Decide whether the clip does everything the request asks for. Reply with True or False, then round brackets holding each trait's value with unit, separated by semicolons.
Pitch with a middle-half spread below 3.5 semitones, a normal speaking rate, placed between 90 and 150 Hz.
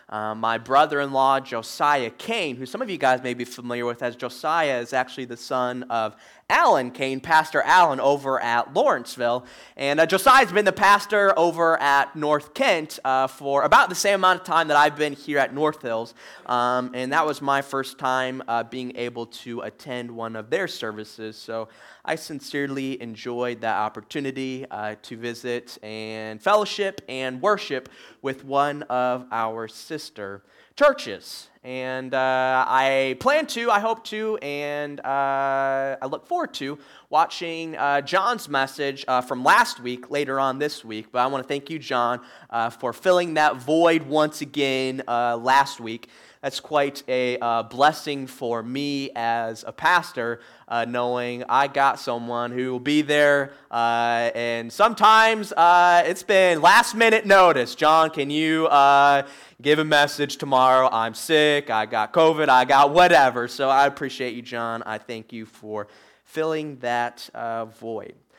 False (4.0 semitones; 165 wpm; 135 Hz)